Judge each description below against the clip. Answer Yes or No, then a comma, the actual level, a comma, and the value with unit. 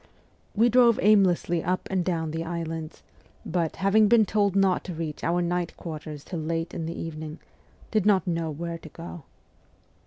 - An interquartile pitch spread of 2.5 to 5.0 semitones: Yes, average, 2.9 semitones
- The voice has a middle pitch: Yes, medium, 170 Hz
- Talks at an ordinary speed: Yes, average, 175 wpm